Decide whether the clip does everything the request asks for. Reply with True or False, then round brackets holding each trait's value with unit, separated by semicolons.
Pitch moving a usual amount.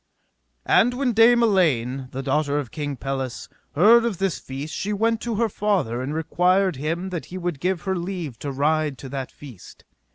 False (6.2 semitones)